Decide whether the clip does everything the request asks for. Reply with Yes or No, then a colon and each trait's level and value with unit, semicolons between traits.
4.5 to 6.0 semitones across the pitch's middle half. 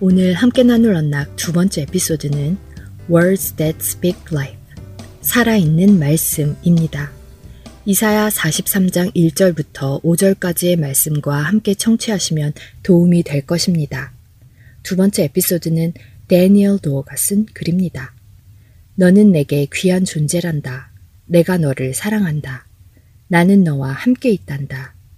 Yes: average, 5.3 semitones